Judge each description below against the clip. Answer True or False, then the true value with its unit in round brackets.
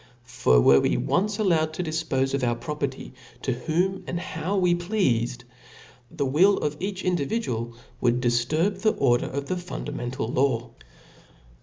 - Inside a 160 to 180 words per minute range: False (150 wpm)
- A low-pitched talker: False (145 Hz)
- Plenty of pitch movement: True (6.7 semitones)